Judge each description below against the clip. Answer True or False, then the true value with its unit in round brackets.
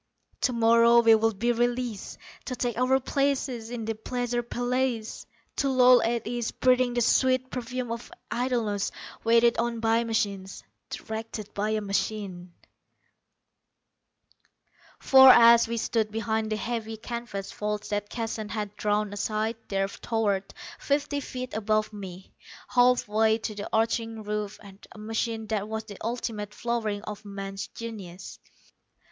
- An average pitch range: False (2.3 semitones)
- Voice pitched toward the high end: True (225 Hz)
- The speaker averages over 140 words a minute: False (135 wpm)